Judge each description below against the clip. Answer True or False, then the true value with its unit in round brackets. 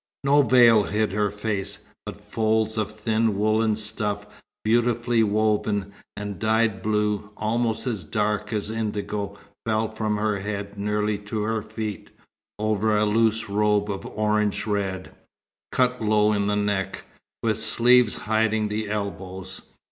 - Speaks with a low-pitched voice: True (105 Hz)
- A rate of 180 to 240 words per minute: False (140 wpm)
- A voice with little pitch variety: True (1.1 semitones)